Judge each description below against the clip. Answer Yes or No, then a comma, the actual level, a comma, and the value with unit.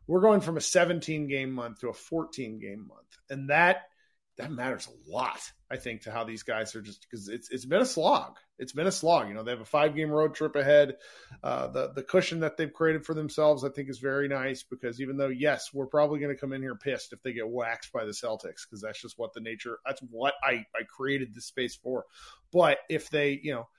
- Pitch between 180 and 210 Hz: No, medium, 140 Hz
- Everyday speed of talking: No, fast, 245 wpm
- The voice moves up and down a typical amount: Yes, average, 3.6 semitones